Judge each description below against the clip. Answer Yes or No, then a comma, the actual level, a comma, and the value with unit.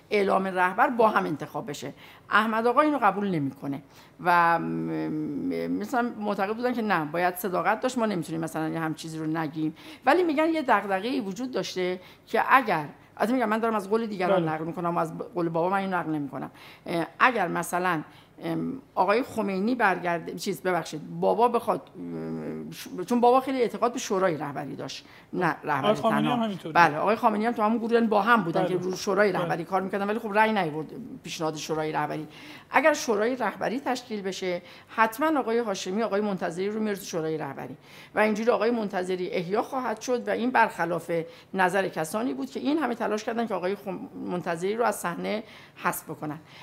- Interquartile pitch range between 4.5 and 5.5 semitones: Yes, average, 5.1 semitones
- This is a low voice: No, high, 190 Hz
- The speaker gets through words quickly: Yes, fast, 170 wpm